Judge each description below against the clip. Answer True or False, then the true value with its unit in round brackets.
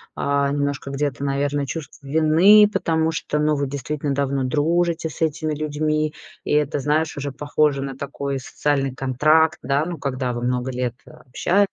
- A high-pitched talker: False (145 Hz)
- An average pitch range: False (2.1 semitones)